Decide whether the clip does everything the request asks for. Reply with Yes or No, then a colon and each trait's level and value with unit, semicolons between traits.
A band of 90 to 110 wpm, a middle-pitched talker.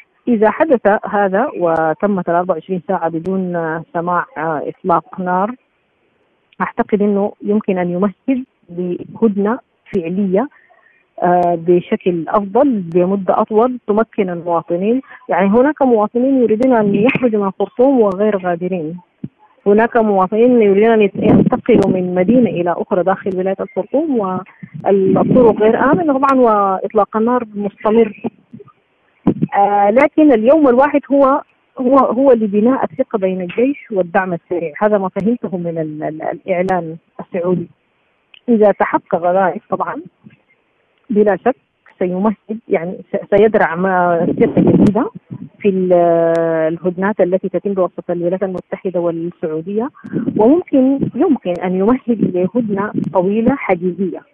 No: average, 105 wpm; high, 200 Hz